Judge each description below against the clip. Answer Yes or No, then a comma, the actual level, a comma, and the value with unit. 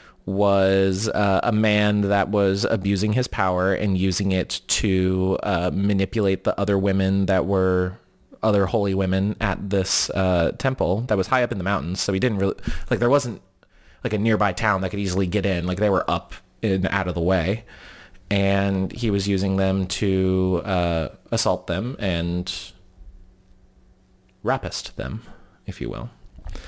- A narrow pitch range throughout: Yes, narrow, 1.5 semitones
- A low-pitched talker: Yes, very low, 95 Hz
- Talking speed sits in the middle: Yes, average, 165 wpm